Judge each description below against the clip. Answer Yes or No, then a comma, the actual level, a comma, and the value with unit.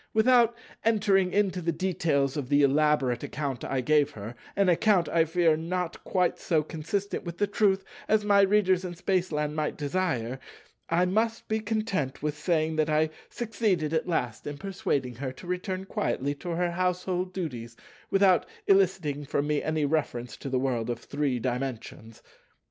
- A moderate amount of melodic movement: Yes, average, 4.9 semitones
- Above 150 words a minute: Yes, average, 160 wpm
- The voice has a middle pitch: Yes, medium, 165 Hz